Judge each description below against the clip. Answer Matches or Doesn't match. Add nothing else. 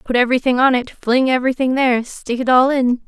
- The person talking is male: Doesn't match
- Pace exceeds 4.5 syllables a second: Matches